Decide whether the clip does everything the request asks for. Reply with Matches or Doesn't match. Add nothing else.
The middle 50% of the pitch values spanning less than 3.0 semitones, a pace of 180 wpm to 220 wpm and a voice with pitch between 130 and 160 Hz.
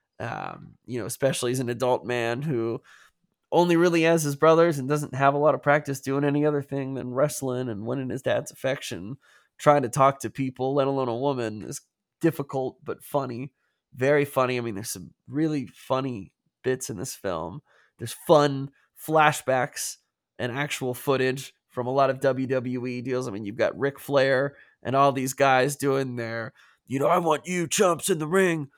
Matches